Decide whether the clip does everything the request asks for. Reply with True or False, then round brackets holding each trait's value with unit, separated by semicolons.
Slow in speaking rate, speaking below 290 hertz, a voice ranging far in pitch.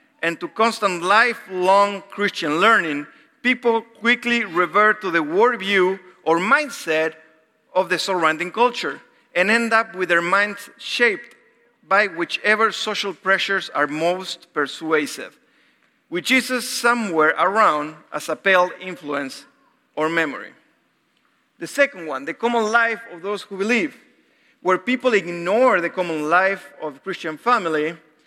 True (130 wpm; 190 Hz; 5.7 semitones)